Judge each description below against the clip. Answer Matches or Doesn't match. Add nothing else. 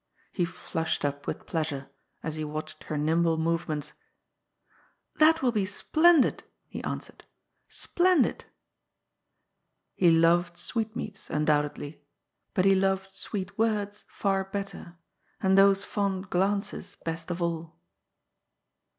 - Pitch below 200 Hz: Matches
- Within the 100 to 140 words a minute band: Matches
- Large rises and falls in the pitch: Doesn't match